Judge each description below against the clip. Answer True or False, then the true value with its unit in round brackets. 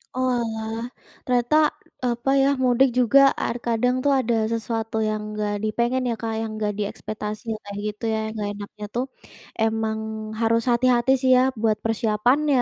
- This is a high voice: True (230 Hz)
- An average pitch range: False (2.3 semitones)